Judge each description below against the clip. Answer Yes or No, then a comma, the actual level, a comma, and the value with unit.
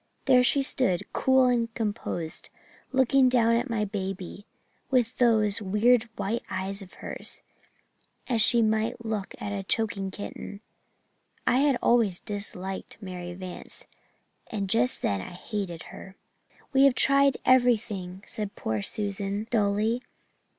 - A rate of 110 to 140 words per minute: Yes, slow, 135 wpm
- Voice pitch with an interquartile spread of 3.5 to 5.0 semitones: Yes, average, 3.9 semitones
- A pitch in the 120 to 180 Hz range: No, high, 215 Hz